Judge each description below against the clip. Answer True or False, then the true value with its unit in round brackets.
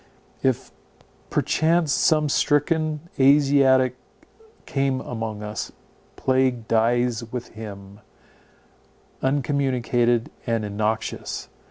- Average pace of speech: False (75 wpm)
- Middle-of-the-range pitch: False (125 Hz)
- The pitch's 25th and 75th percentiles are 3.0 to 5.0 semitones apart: True (3.8 semitones)